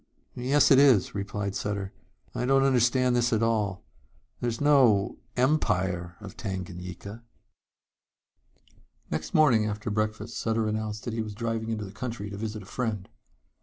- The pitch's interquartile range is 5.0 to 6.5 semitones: No, average, 3.2 semitones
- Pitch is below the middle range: Yes, low, 110 Hz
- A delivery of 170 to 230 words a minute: No, average, 145 wpm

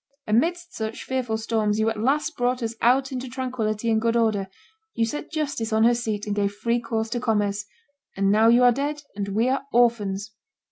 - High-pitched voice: Yes, high, 230 Hz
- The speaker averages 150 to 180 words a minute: No, average, 200 wpm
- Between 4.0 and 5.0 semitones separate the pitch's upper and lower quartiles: No, average, 2.7 semitones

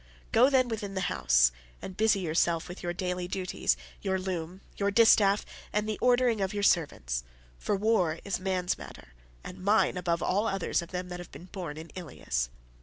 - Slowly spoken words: No, average, 185 wpm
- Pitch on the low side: No, medium, 185 Hz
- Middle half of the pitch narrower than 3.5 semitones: Yes, average, 3.0 semitones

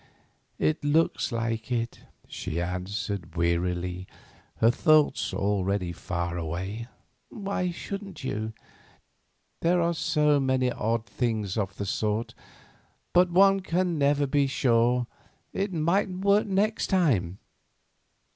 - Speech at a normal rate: No, slow, 115 wpm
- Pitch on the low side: Yes, low, 125 Hz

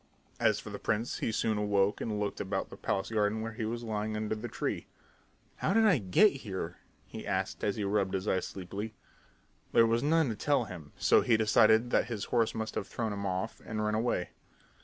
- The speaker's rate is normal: No, fast, 215 wpm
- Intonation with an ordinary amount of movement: No, narrow, 2.1 semitones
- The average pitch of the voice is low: Yes, low, 110 Hz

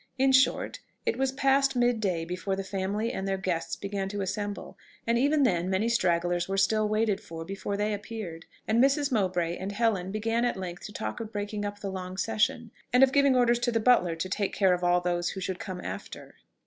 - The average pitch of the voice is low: No, high, 205 Hz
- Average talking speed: No, fast, 220 wpm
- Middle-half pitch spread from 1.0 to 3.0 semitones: No, average, 3.9 semitones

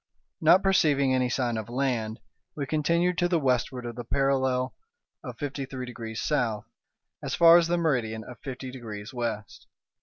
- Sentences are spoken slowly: No, average, 170 wpm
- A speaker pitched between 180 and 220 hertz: No, low, 130 Hz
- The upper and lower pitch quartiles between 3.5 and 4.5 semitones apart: Yes, average, 3.9 semitones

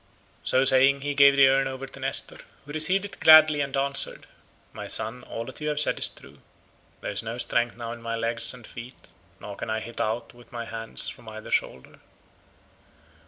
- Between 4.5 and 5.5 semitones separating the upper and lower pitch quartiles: No, average, 3.3 semitones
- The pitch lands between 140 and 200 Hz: No, low, 125 Hz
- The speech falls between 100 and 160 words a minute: No, fast, 205 wpm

